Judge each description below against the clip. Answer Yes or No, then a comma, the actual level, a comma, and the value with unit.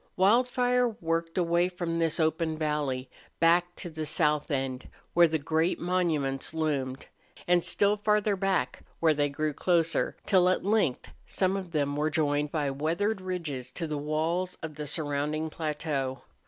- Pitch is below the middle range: No, medium, 160 Hz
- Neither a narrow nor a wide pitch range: Yes, average, 3.4 semitones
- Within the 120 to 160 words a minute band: Yes, average, 155 wpm